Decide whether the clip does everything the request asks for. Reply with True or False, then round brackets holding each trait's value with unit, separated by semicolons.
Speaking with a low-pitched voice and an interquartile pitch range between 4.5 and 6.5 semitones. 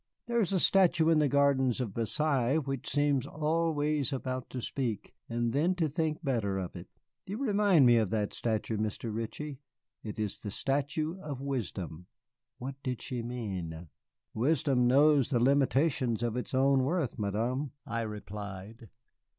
True (130 Hz; 4.9 semitones)